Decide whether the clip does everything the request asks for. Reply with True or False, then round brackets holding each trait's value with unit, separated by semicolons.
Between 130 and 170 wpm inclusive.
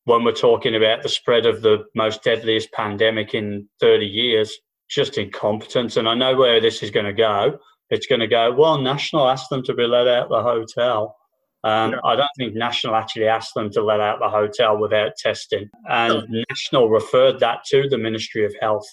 False (200 wpm)